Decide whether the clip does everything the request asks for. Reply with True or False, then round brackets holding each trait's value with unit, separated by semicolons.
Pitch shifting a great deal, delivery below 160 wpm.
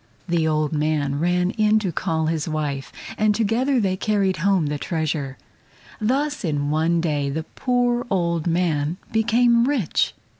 True (5.8 semitones; 150 wpm)